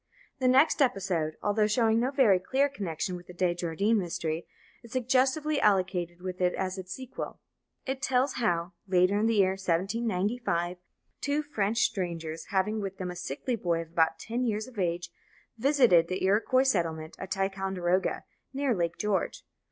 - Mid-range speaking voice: No, high, 195 Hz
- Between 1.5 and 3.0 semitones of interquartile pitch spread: No, average, 5.1 semitones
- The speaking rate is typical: Yes, average, 165 wpm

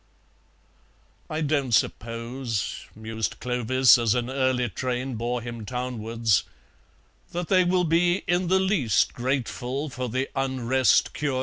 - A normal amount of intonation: Yes, average, 3.3 semitones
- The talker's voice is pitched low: Yes, low, 130 Hz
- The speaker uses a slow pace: Yes, slow, 125 wpm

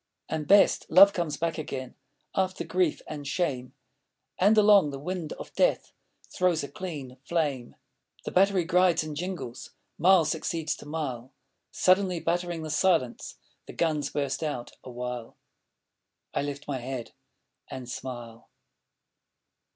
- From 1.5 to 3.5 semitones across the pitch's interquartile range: No, average, 5.3 semitones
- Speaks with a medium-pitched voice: Yes, medium, 155 Hz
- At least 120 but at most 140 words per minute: Yes, slow, 135 wpm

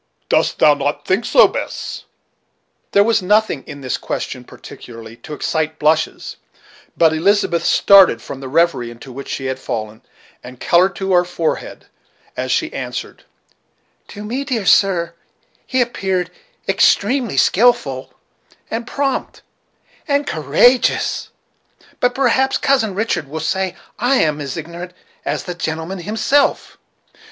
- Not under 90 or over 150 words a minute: Yes, slow, 135 wpm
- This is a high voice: No, medium, 175 Hz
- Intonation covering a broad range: Yes, wide, 6.8 semitones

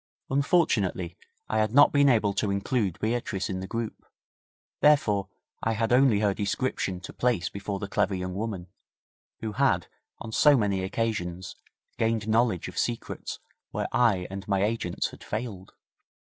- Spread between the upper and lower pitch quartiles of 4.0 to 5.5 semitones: No, average, 3.1 semitones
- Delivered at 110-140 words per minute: No, average, 155 wpm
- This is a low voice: Yes, low, 105 Hz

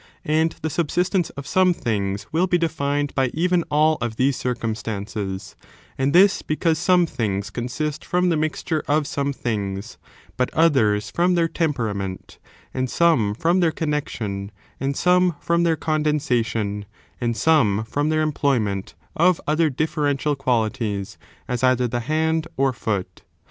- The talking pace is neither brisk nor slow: Yes, average, 150 wpm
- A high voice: No, medium, 140 Hz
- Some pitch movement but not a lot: No, wide, 6.2 semitones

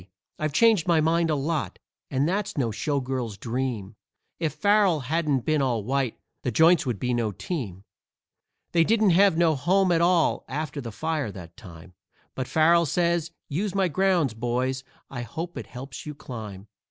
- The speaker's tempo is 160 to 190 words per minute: Yes, average, 170 wpm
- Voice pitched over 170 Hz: No, medium, 145 Hz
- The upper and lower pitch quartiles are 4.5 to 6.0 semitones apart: Yes, wide, 5.6 semitones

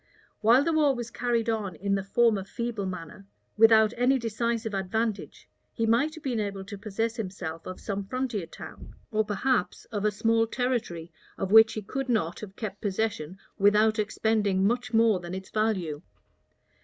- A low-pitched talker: No, high, 215 Hz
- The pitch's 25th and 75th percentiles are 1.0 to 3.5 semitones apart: Yes, average, 3.0 semitones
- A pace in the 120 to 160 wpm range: No, average, 170 wpm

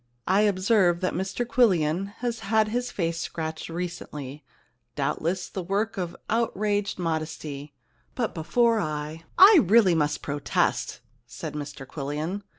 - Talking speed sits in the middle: No, slow, 130 wpm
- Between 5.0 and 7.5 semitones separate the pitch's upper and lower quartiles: Yes, average, 5.3 semitones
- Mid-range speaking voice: Yes, medium, 180 Hz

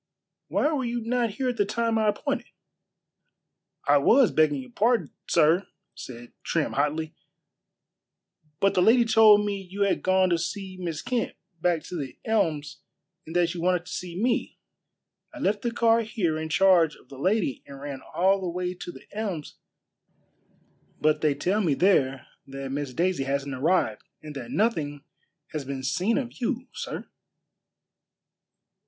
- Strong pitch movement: Yes, wide, 6.5 semitones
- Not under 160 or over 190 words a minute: Yes, average, 165 wpm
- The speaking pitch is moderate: Yes, medium, 180 Hz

